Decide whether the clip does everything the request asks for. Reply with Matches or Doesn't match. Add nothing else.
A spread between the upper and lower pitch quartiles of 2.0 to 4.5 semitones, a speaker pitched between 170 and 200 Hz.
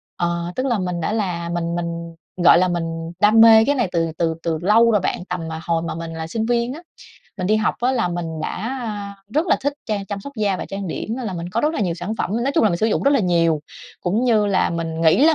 Doesn't match